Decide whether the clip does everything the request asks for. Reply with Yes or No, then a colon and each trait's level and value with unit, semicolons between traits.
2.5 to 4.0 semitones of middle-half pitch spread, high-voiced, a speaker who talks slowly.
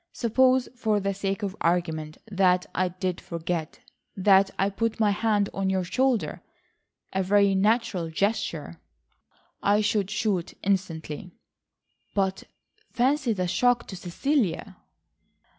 Yes: average, 3.2 semitones; high, 195 Hz; slow, 115 wpm